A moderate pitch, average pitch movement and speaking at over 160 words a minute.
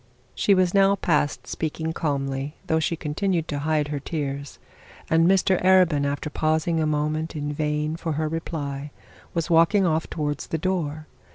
No: medium, 155 Hz; narrow, 2.2 semitones; average, 170 wpm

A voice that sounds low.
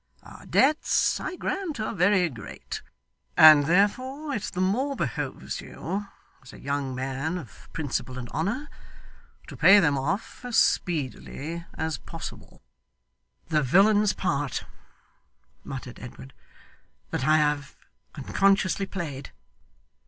No: medium, 165 Hz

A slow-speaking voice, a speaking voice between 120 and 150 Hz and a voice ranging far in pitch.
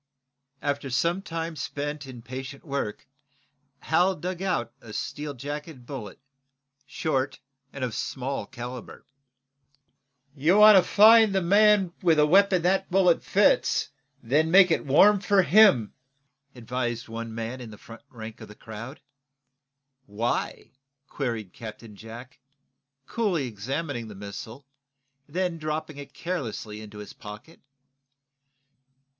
Yes: slow, 130 wpm; medium, 140 Hz; wide, 6.8 semitones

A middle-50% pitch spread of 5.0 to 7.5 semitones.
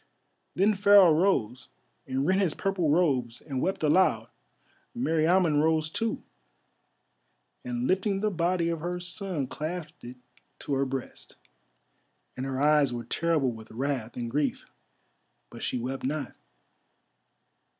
Yes: wide, 5.4 semitones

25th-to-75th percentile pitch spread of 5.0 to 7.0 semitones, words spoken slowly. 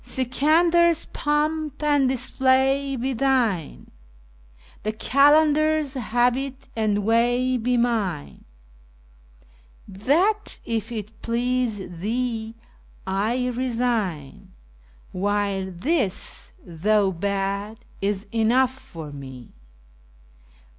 Yes: average, 5.3 semitones; slow, 80 wpm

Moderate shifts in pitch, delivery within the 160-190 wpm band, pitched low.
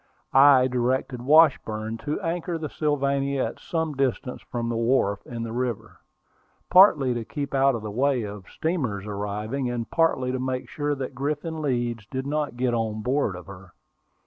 Yes: average, 3.9 semitones; average, 170 wpm; low, 130 Hz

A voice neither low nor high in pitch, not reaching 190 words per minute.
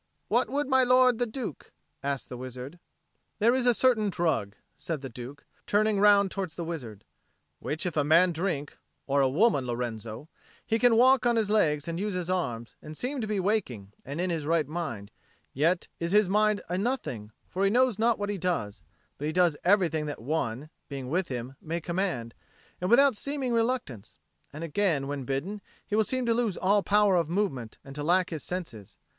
No: medium, 175 Hz; average, 195 wpm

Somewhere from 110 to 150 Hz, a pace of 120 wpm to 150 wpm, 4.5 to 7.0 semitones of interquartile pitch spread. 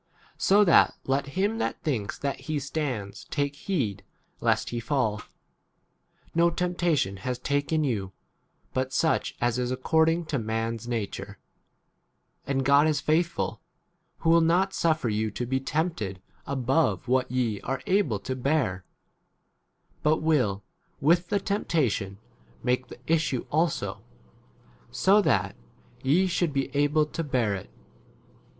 Yes: medium, 140 Hz; average, 145 wpm; average, 5.1 semitones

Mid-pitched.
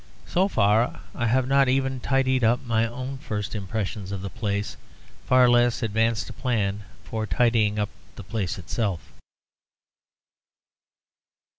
No: low, 115 Hz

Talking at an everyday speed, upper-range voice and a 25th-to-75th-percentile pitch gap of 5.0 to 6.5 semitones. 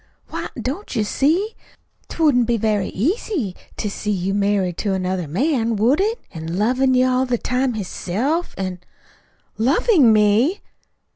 Yes: average, 155 wpm; high, 230 Hz; wide, 5.6 semitones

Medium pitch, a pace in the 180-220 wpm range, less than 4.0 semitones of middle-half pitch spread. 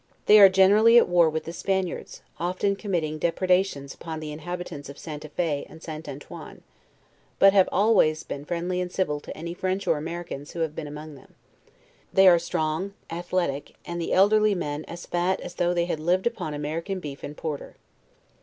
Yes: medium, 170 Hz; average, 190 wpm; average, 3.3 semitones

